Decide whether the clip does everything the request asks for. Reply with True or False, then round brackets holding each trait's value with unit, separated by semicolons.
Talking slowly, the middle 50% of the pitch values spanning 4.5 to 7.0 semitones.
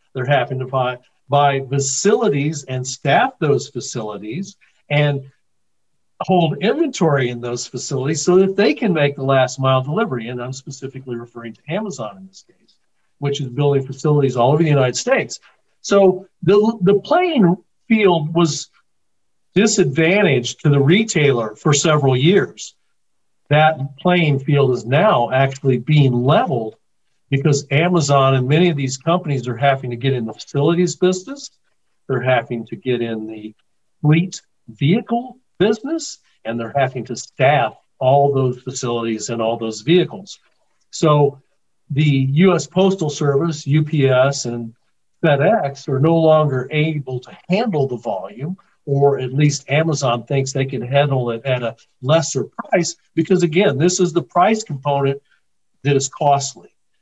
False (145 wpm; 4.8 semitones)